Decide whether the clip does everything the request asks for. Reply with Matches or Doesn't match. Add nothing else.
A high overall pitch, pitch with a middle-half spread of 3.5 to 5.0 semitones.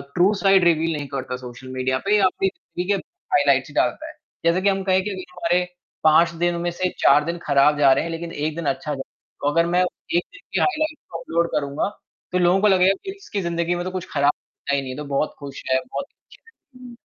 Doesn't match